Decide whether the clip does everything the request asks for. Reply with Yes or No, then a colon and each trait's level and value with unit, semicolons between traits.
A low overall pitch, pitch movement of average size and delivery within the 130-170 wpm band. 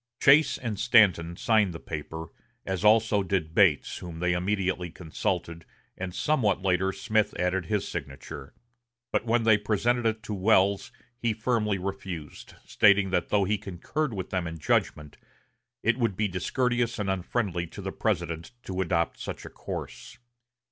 Yes: very low, 95 Hz; average, 3.8 semitones; average, 155 wpm